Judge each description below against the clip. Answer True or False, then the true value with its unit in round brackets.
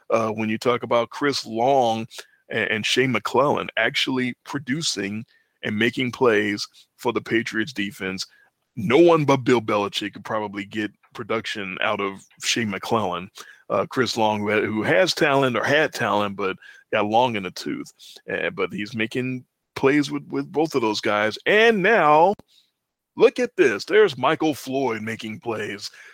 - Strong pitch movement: False (4.9 semitones)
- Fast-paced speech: False (160 wpm)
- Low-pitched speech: True (120 Hz)